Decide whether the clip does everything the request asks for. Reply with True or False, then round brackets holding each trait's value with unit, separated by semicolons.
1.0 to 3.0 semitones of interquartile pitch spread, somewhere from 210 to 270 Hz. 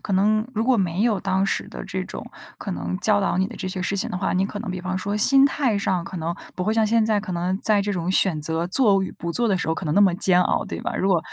False (2.7 semitones; 190 Hz)